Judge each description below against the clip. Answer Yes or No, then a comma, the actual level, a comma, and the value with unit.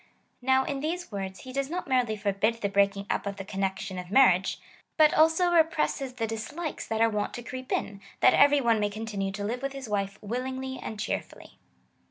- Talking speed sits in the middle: No, fast, 215 wpm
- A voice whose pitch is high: Yes, high, 230 Hz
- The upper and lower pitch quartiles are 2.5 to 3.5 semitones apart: No, average, 5.2 semitones